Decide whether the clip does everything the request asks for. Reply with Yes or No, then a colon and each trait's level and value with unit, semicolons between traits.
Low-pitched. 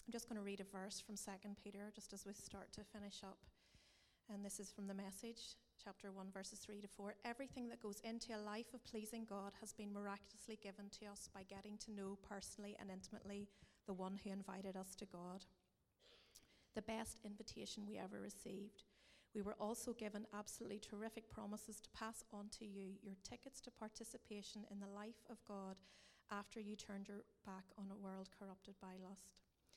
No: high, 205 Hz